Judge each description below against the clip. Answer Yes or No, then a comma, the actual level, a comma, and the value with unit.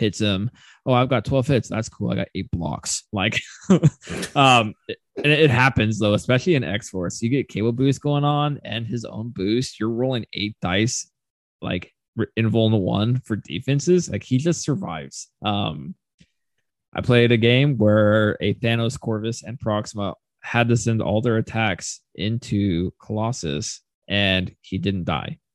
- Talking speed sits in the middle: Yes, average, 165 wpm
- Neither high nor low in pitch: No, low, 110 Hz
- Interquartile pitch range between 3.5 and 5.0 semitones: Yes, average, 3.9 semitones